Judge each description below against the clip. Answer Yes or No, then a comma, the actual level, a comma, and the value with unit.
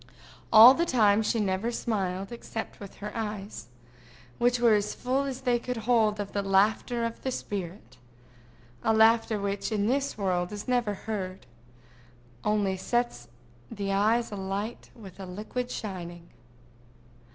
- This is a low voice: No, high, 210 Hz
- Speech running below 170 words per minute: Yes, average, 140 wpm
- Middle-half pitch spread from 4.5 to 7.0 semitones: No, average, 3.4 semitones